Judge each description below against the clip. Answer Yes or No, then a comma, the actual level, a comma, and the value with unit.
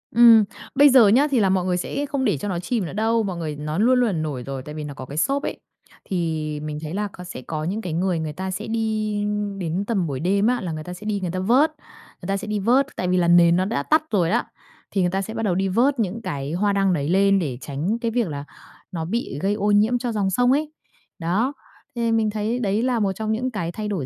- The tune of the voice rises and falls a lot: No, average, 4.9 semitones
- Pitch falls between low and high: No, high, 195 Hz